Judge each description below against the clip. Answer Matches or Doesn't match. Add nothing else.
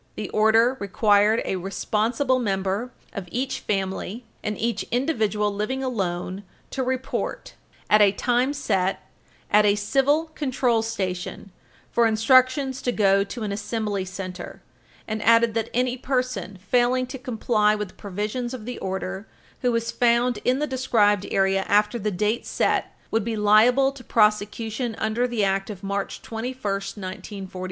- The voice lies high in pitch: Matches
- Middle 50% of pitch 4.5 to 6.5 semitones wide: Doesn't match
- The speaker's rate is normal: Matches